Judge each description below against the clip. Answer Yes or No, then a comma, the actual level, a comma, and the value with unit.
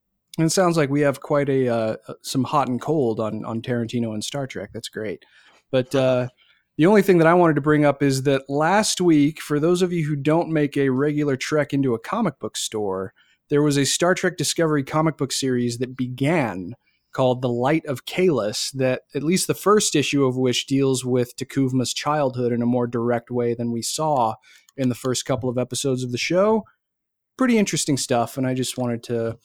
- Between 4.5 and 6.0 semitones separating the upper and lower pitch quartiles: No, average, 3.6 semitones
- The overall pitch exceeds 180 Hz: No, low, 135 Hz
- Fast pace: Yes, fast, 210 wpm